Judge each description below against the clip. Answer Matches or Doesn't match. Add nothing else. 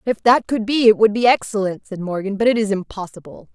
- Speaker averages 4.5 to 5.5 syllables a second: Doesn't match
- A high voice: Matches